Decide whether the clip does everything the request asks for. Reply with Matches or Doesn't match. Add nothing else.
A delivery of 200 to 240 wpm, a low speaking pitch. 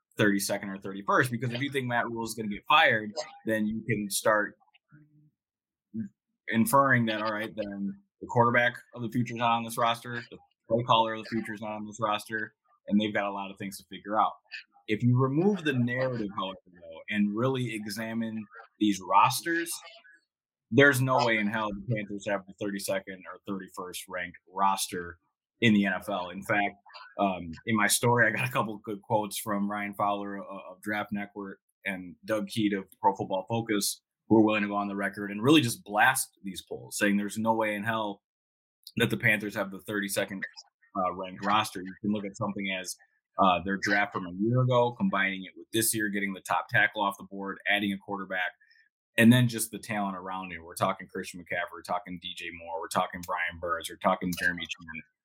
Matches